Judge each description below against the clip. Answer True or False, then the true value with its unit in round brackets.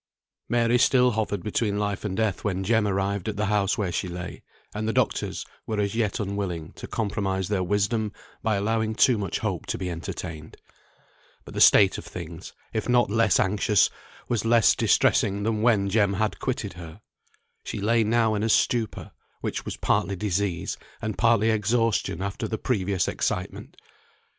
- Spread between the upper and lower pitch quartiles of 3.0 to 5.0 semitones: False (2.5 semitones)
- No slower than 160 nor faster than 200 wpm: True (170 wpm)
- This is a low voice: True (105 Hz)